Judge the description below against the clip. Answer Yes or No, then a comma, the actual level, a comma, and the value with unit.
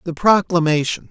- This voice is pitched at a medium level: Yes, medium, 170 Hz